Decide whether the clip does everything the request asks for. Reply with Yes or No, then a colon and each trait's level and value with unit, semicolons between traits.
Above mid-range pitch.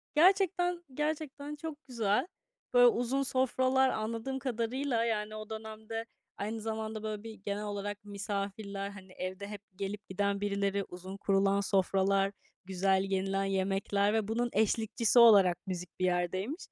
Yes: high, 210 Hz